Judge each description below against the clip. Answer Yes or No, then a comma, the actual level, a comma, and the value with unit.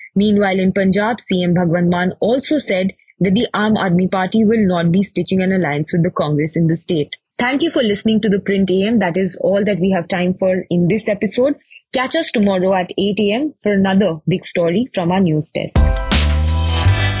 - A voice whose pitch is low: No, high, 190 Hz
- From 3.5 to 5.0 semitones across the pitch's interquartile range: No, average, 3.1 semitones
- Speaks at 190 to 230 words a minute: Yes, average, 200 wpm